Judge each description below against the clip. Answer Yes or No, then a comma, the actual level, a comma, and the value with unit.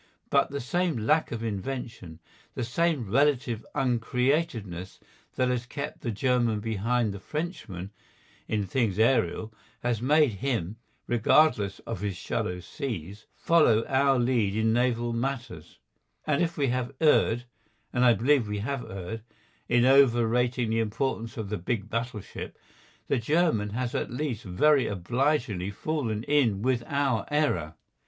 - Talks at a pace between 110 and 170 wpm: Yes, average, 140 wpm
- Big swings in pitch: No, average, 4.2 semitones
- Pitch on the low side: Yes, low, 120 Hz